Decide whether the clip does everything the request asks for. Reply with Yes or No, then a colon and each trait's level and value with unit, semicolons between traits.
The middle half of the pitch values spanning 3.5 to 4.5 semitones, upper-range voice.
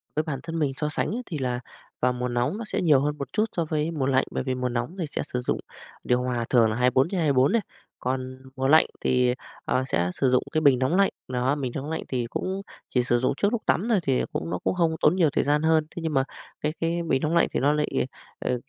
No: average, 4.1 semitones; medium, 140 Hz